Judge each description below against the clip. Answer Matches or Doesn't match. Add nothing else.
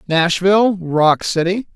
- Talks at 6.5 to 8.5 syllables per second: Doesn't match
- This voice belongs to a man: Matches